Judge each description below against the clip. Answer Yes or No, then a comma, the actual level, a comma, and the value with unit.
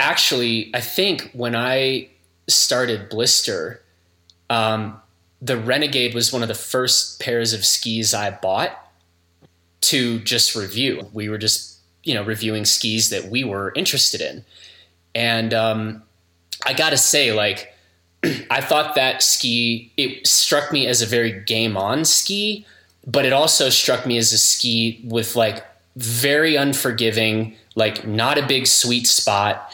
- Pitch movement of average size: Yes, average, 3.1 semitones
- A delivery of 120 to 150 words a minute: Yes, average, 145 wpm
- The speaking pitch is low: Yes, low, 115 Hz